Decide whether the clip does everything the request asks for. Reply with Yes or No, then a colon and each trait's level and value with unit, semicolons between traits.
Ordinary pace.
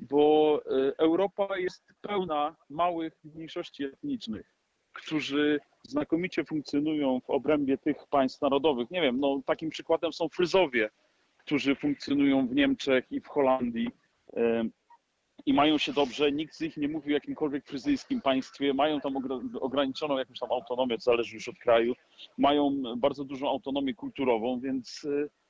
Yes: average, 140 wpm